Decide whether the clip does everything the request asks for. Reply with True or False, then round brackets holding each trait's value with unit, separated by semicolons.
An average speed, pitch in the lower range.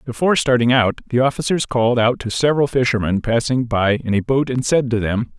False (210 wpm; 120 Hz)